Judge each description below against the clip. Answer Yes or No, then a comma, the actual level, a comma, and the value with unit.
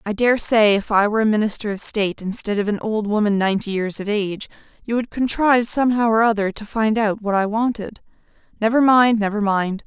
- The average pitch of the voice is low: No, high, 215 Hz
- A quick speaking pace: Yes, fast, 215 wpm